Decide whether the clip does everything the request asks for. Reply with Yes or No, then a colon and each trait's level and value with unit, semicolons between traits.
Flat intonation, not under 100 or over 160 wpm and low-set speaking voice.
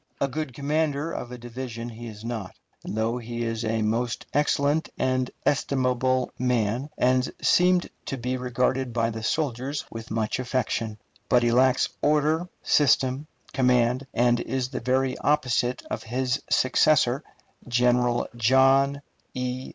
Yes: narrow, 2.3 semitones; average, 140 wpm; low, 125 Hz